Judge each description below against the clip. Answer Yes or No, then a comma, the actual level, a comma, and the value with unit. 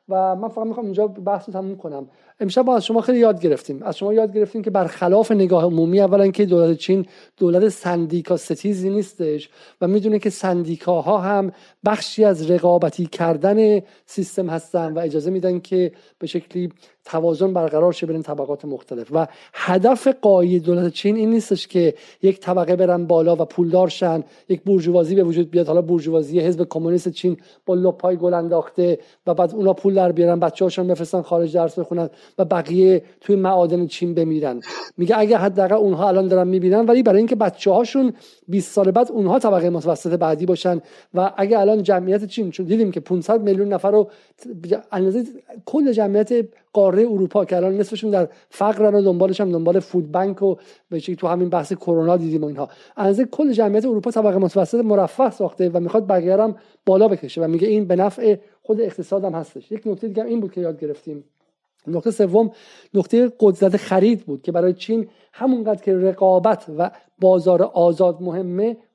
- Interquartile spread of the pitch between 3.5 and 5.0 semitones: No, average, 3.1 semitones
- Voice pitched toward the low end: No, medium, 185 Hz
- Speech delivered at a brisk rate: Yes, fast, 175 wpm